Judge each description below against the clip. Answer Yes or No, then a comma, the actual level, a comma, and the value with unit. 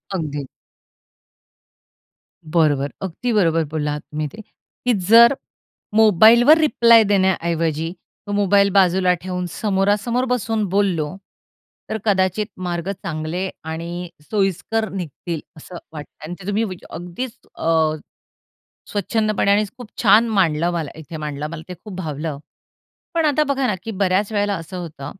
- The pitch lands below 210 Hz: Yes, medium, 185 Hz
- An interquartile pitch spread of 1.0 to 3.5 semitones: No, average, 4.6 semitones